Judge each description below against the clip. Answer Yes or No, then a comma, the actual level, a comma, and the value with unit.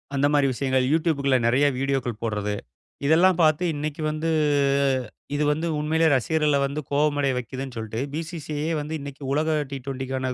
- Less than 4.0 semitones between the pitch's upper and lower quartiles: Yes, average, 2.8 semitones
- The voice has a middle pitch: Yes, medium, 145 Hz